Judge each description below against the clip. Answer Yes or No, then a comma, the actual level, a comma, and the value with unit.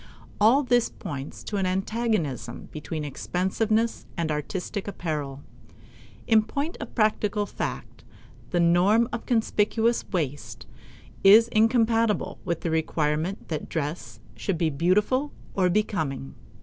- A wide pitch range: Yes, wide, 6.1 semitones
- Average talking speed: No, slow, 120 wpm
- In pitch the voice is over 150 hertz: Yes, high, 190 Hz